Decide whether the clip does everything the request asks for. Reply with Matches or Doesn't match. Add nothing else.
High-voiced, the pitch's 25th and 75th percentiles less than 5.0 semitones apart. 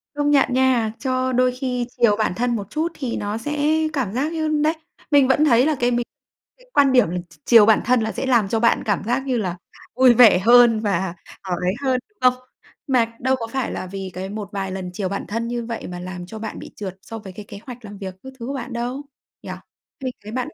Matches